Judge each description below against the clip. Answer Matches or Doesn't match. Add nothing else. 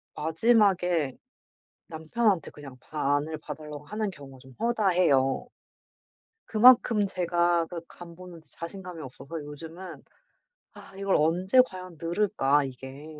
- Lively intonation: Doesn't match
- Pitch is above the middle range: Doesn't match